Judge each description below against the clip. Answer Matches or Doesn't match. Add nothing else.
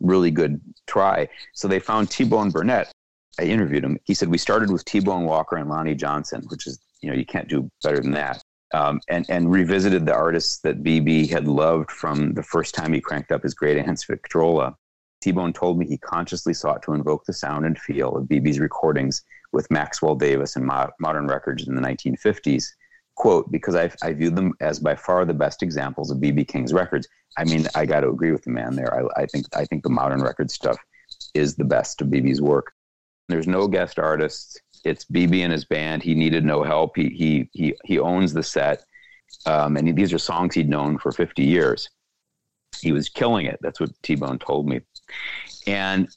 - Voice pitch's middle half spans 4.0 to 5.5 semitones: Doesn't match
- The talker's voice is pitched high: Doesn't match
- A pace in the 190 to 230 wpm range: Matches